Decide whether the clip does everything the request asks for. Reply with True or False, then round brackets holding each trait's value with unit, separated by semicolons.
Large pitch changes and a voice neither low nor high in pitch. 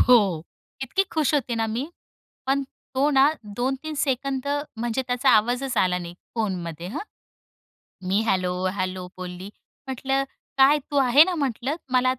False (6.0 semitones; 250 Hz)